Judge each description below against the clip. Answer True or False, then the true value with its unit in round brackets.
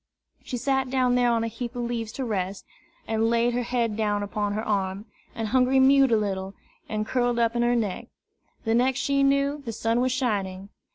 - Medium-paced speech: False (210 wpm)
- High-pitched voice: True (235 Hz)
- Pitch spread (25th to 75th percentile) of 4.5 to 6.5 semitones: False (3.0 semitones)